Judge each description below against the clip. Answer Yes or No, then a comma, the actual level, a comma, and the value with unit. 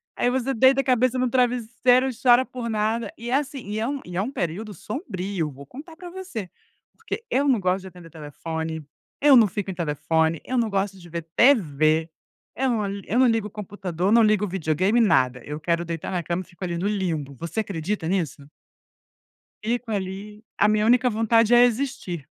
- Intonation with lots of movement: Yes, wide, 6.1 semitones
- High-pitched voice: Yes, high, 210 Hz